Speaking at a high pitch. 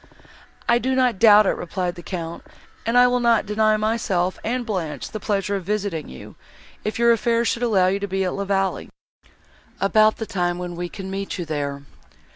Yes: high, 200 Hz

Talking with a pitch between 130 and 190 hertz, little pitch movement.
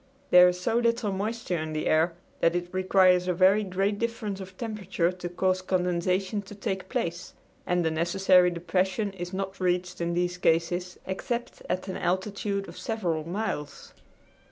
Yes: medium, 185 Hz; narrow, 2.0 semitones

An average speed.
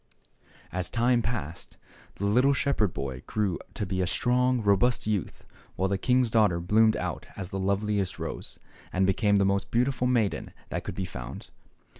Yes: average, 170 wpm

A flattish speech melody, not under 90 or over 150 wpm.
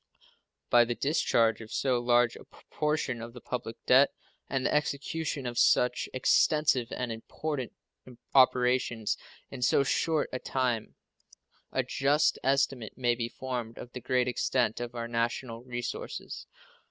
Yes: narrow, 2.2 semitones; average, 140 wpm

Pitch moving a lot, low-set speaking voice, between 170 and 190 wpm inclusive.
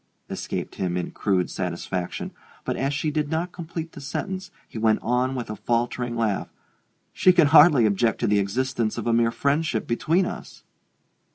Yes: wide, 5.9 semitones; low, 125 Hz; average, 175 wpm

